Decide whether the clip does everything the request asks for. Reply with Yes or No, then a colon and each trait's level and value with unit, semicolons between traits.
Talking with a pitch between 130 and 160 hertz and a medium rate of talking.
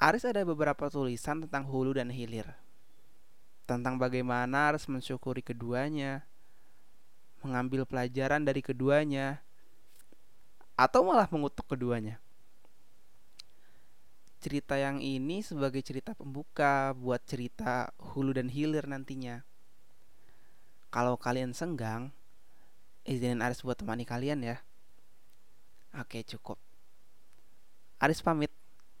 Yes: low, 135 Hz; average, 95 wpm